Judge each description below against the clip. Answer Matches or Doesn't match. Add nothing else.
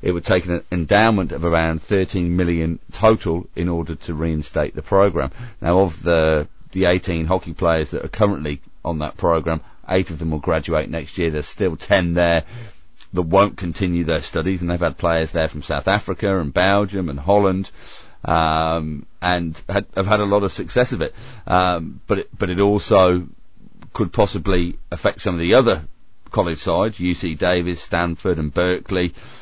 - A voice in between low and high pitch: Doesn't match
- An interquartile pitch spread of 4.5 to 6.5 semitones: Doesn't match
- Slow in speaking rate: Doesn't match